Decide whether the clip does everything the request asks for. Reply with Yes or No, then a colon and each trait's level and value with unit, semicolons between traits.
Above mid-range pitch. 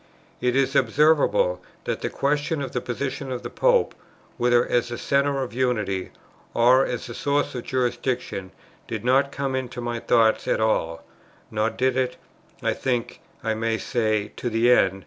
No: low, 125 Hz